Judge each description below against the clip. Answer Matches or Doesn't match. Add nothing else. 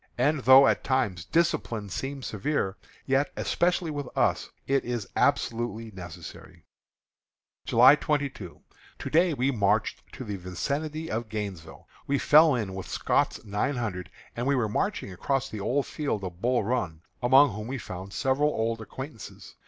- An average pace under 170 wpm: Matches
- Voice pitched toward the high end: Doesn't match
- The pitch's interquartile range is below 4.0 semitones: Doesn't match